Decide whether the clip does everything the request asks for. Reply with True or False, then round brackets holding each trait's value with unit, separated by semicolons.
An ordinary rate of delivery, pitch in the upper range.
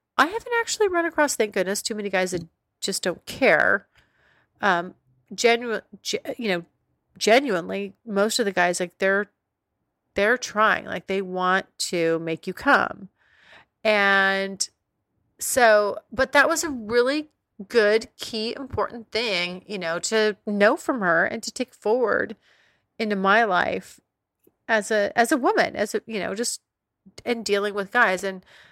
True (155 wpm; 210 Hz)